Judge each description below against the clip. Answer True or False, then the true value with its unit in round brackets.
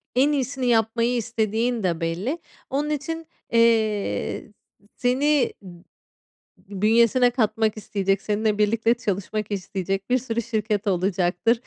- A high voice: True (225 Hz)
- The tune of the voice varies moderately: True (3.3 semitones)